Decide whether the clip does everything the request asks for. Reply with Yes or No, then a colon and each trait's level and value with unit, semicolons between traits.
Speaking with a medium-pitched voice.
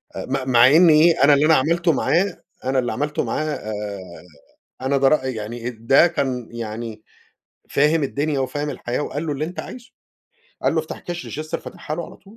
Yes: medium, 145 Hz